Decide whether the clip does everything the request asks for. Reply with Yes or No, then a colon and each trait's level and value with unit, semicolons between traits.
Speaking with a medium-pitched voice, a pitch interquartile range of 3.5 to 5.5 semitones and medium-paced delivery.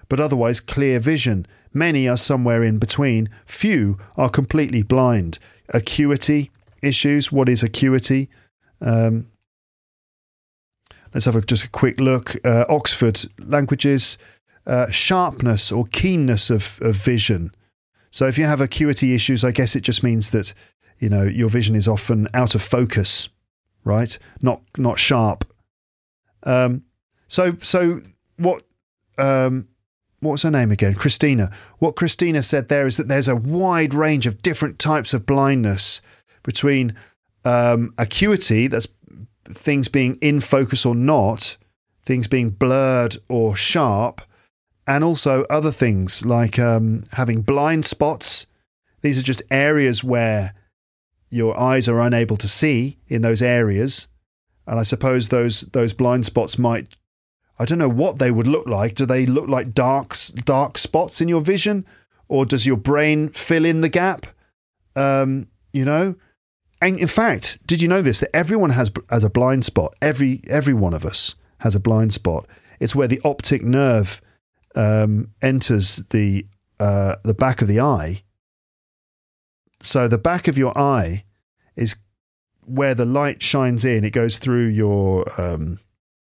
No: low, 125 Hz; average, 4.5 semitones; average, 150 wpm